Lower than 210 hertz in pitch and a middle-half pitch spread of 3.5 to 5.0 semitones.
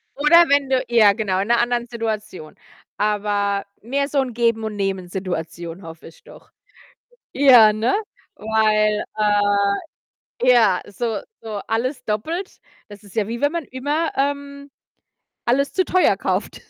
No: high, 225 Hz; average, 4.7 semitones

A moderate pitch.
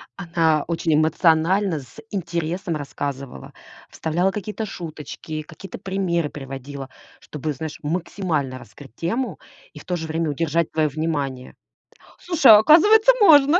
Yes: medium, 165 Hz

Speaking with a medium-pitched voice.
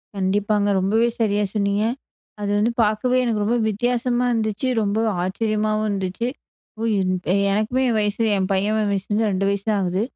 No: high, 210 Hz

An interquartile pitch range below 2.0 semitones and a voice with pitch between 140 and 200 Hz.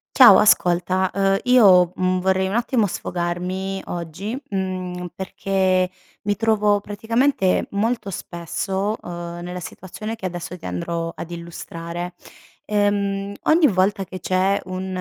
No: narrow, 2.4 semitones; high, 190 Hz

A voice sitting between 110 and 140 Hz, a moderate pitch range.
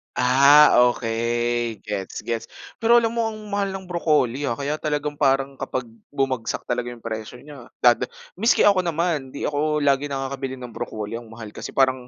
Yes: low, 135 Hz; average, 4.0 semitones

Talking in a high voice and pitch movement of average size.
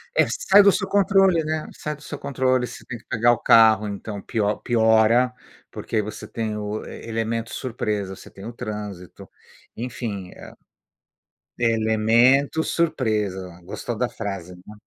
No: low, 115 Hz; average, 3.6 semitones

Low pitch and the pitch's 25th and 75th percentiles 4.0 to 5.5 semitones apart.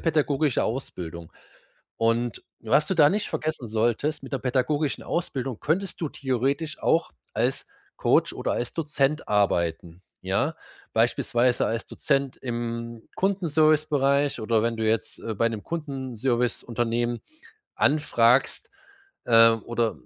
Yes: low, 125 Hz; average, 4.5 semitones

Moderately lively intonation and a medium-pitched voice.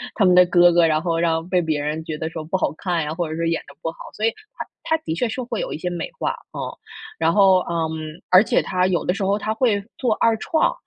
Yes: average, 3.6 semitones; medium, 175 Hz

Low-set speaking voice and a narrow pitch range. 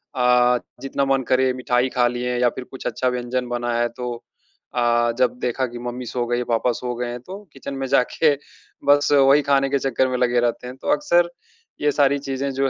Yes: low, 125 Hz; narrow, 1.9 semitones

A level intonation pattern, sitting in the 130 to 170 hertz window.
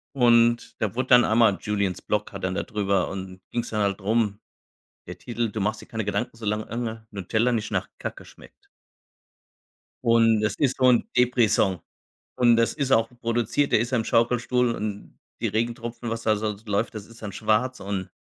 No: narrow, 2.2 semitones; low, 115 Hz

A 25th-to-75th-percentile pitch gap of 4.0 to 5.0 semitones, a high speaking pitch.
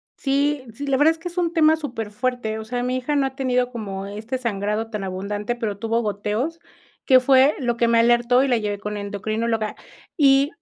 Yes: average, 4.3 semitones; high, 240 Hz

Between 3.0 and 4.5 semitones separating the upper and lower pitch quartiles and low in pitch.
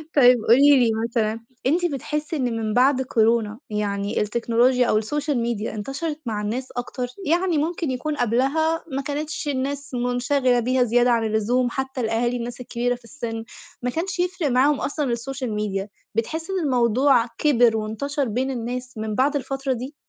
No: average, 3.6 semitones; very high, 250 Hz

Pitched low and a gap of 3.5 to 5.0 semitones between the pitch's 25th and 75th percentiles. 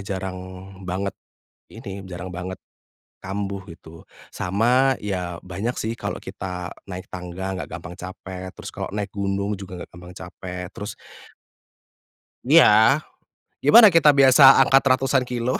Yes: very low, 95 Hz; average, 4.6 semitones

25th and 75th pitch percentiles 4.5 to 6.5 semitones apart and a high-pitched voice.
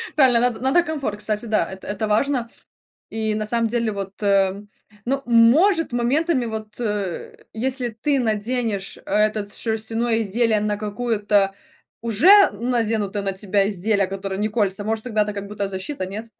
No: average, 2.9 semitones; high, 220 Hz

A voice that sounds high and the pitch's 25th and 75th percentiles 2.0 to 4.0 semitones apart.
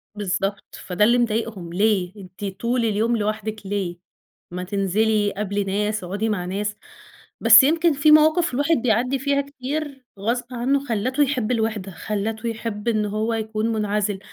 Yes: high, 220 Hz; average, 3.3 semitones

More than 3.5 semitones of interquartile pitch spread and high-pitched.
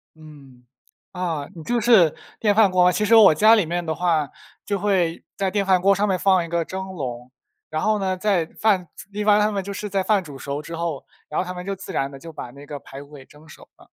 No: average, 4.5 semitones; medium, 180 Hz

